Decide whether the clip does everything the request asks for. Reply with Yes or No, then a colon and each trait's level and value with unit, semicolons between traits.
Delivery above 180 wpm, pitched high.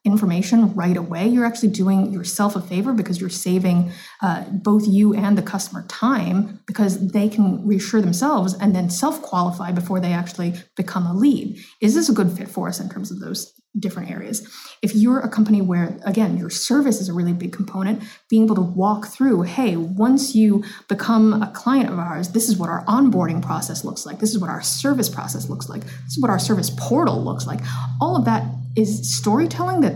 Yes: fast, 205 wpm; high, 195 Hz